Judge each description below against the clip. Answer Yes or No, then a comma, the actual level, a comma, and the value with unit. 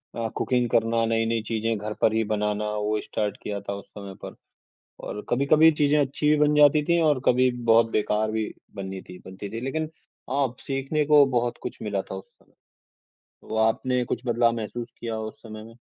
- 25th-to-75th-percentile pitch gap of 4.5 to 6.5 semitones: No, average, 3.9 semitones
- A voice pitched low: Yes, low, 115 Hz